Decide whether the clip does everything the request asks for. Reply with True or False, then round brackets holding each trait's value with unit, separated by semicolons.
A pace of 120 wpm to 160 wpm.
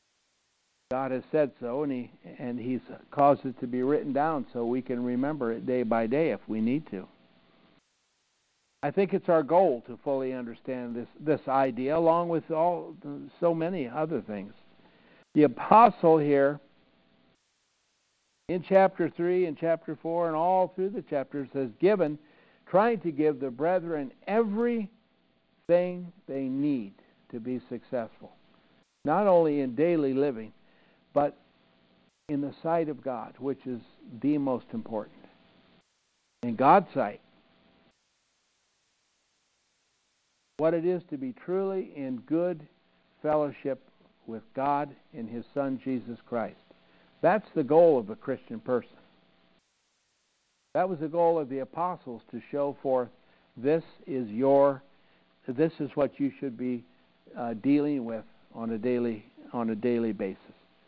True (140 wpm)